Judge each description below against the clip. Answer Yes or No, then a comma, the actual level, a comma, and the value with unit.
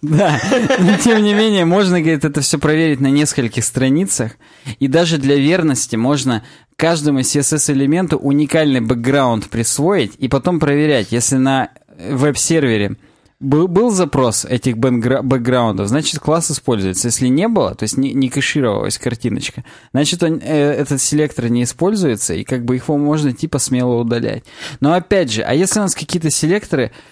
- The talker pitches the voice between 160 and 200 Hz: No, medium, 140 Hz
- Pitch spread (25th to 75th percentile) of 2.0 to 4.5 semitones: Yes, average, 4.0 semitones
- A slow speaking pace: No, average, 155 wpm